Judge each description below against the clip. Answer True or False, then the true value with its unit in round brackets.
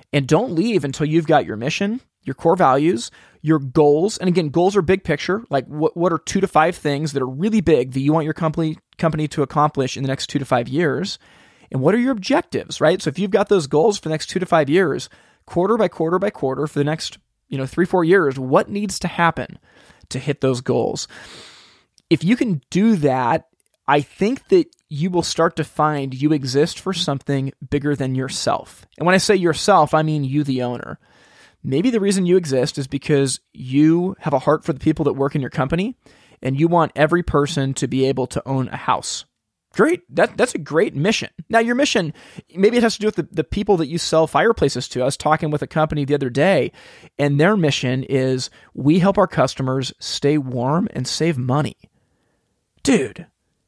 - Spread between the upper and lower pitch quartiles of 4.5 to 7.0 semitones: True (4.8 semitones)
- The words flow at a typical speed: False (215 wpm)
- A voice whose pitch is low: False (155 Hz)